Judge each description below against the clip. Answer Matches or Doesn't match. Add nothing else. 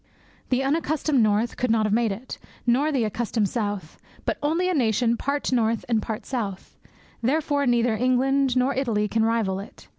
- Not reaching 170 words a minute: Doesn't match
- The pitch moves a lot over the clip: Doesn't match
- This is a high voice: Matches